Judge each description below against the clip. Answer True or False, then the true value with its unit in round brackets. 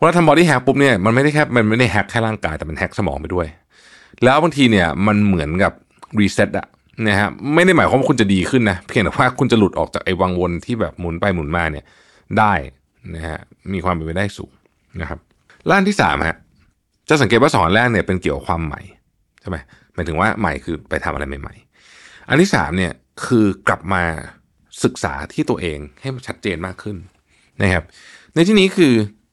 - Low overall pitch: True (100 Hz)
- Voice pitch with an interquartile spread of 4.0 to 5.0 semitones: False (5.5 semitones)